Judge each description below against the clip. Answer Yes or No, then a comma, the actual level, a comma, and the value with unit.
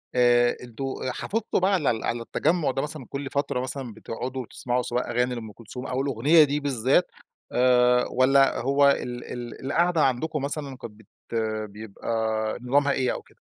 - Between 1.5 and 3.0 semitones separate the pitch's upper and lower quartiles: Yes, average, 2.7 semitones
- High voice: No, low, 130 Hz